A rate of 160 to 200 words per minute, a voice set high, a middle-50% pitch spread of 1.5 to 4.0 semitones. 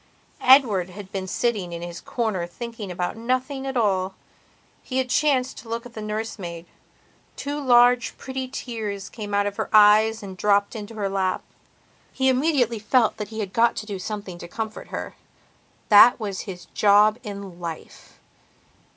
Yes: average, 170 wpm; high, 215 Hz; average, 3.7 semitones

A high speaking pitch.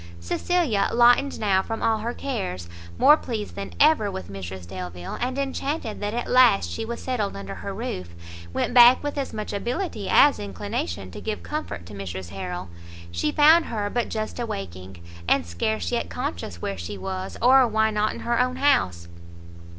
Yes: high, 205 Hz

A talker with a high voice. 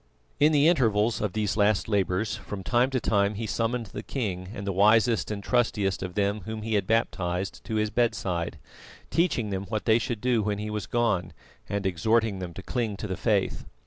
No: low, 105 Hz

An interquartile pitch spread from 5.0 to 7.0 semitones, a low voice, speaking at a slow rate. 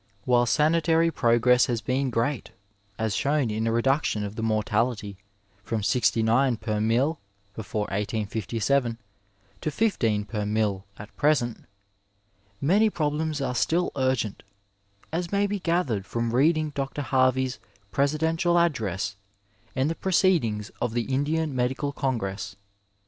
Yes: wide, 5.4 semitones; low, 125 Hz; slow, 130 wpm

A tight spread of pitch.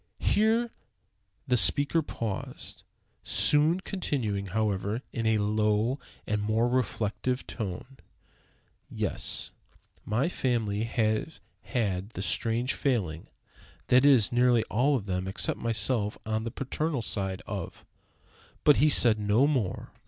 No: average, 4.2 semitones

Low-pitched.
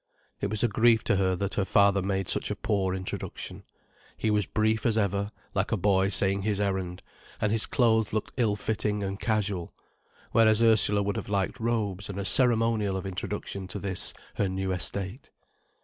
Yes: low, 100 Hz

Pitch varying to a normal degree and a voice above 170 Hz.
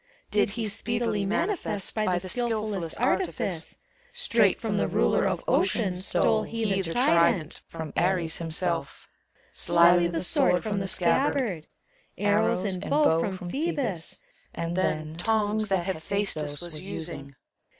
Yes: average, 4.3 semitones; high, 190 Hz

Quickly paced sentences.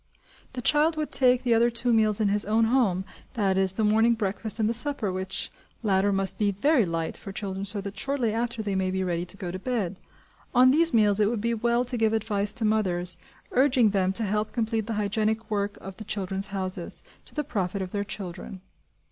Yes: fast, 220 wpm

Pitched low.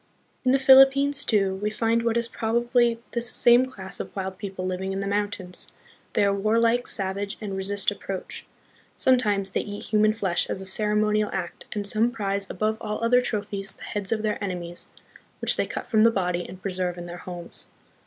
No: high, 205 Hz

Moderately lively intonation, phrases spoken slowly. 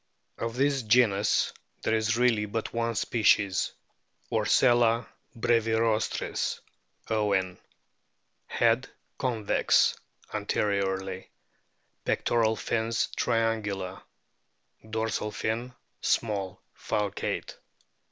No: narrow, 2.1 semitones; slow, 75 wpm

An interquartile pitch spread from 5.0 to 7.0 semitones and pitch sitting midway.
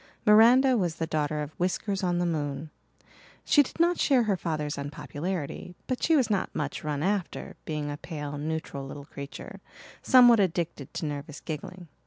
Yes: wide, 5.5 semitones; medium, 165 Hz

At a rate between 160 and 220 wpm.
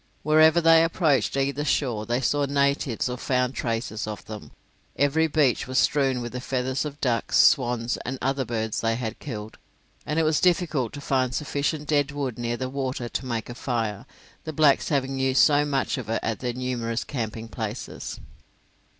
Yes: average, 185 wpm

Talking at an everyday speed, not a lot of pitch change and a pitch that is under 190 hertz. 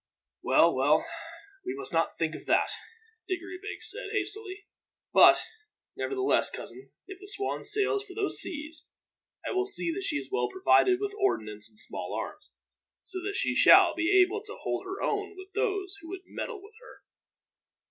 No: average, 175 wpm; narrow, 1.6 semitones; very high, 390 Hz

